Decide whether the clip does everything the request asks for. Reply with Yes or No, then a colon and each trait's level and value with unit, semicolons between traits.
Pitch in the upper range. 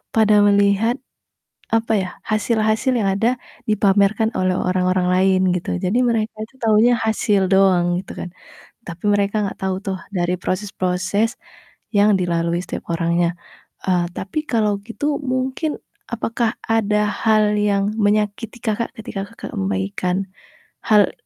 Yes: high, 205 Hz